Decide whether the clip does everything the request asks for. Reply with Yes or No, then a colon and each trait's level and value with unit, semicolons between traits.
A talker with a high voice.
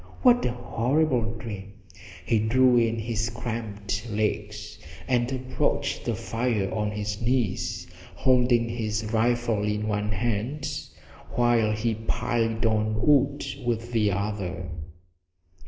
No: low, 115 Hz